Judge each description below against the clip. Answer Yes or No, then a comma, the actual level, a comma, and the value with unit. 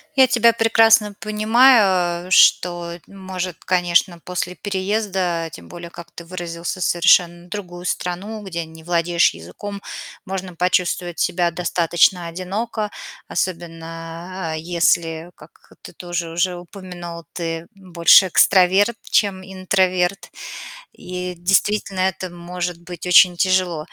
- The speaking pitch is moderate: Yes, medium, 180 Hz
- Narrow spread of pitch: Yes, narrow, 1.9 semitones